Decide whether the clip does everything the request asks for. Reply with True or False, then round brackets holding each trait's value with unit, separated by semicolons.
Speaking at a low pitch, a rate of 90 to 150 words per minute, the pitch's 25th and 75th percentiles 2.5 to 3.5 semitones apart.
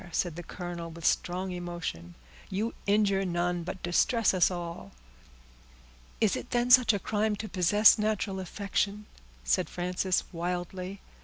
False (185 Hz; 140 wpm; 2.9 semitones)